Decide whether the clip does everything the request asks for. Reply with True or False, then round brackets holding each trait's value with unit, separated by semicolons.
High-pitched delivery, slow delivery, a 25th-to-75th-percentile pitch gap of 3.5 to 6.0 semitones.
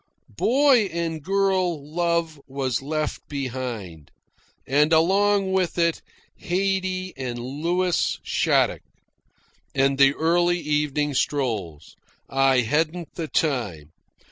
False (155 Hz; 100 wpm; 4.7 semitones)